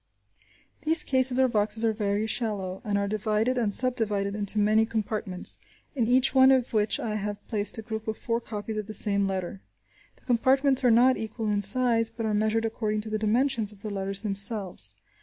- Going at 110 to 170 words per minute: No, average, 195 wpm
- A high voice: Yes, high, 220 Hz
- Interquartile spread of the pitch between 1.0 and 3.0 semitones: Yes, narrow, 2.4 semitones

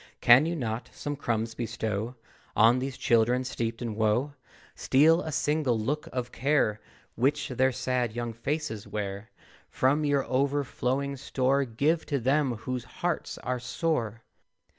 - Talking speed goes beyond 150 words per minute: No, average, 140 wpm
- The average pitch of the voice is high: No, low, 125 Hz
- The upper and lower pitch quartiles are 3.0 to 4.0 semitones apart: Yes, average, 3.5 semitones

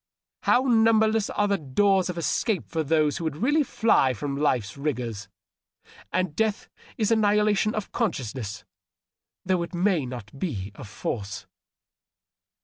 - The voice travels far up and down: Yes, wide, 8.5 semitones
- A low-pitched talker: No, medium, 170 Hz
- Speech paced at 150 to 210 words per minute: No, average, 140 wpm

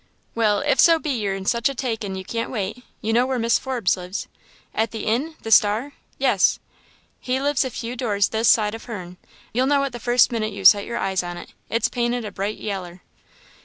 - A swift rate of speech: Yes, fast, 220 wpm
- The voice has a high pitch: Yes, high, 225 Hz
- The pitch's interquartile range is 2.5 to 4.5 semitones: Yes, average, 3.6 semitones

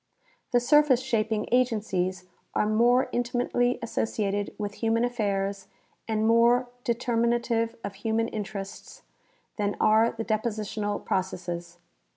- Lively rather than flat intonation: No, average, 2.7 semitones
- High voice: Yes, high, 220 Hz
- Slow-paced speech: Yes, slow, 110 wpm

